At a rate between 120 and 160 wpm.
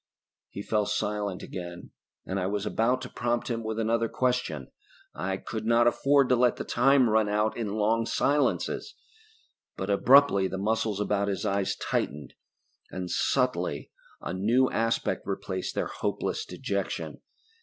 Yes: average, 150 wpm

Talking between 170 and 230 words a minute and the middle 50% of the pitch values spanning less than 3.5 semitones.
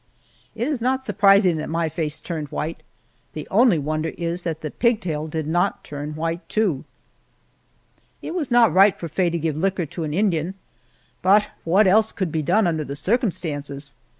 No: average, 180 wpm; average, 4.7 semitones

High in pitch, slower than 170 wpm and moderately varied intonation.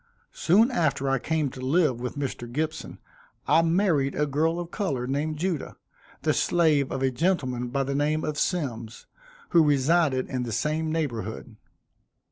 No: medium, 145 Hz; average, 160 wpm; average, 3.9 semitones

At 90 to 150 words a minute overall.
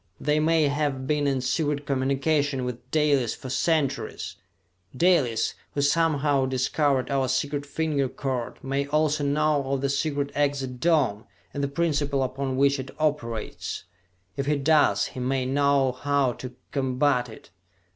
Yes: average, 145 wpm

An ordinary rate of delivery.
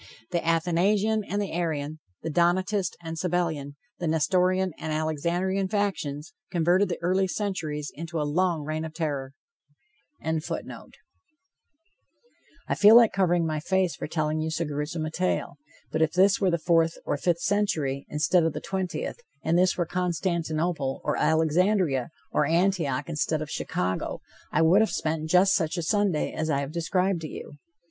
Yes: average, 165 wpm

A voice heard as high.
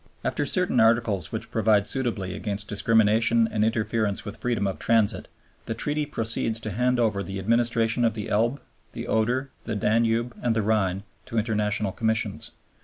No: low, 110 Hz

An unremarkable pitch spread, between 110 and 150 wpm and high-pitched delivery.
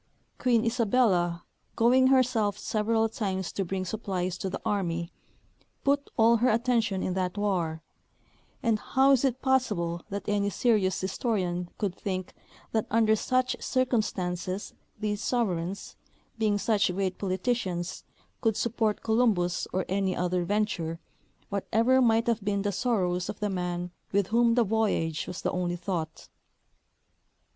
Yes: average, 4.0 semitones; average, 140 wpm; high, 205 Hz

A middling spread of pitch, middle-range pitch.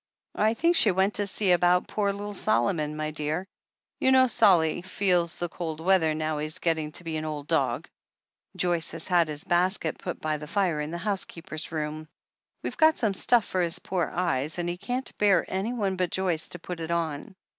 Yes: average, 3.6 semitones; medium, 175 Hz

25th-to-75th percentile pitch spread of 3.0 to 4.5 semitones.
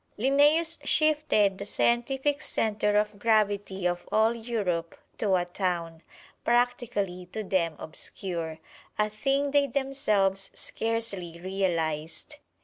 No: average, 5.0 semitones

